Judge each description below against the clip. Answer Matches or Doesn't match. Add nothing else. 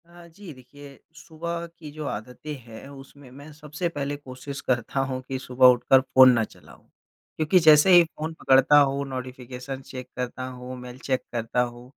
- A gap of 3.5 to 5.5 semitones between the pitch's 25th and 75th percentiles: Doesn't match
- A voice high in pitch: Doesn't match